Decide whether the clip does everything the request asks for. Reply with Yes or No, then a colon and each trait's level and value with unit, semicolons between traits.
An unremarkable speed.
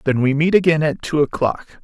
No: fast, 230 wpm